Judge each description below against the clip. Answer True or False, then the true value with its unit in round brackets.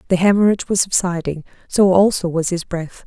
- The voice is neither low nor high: True (180 Hz)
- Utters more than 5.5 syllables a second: True (5.7 syllables/s)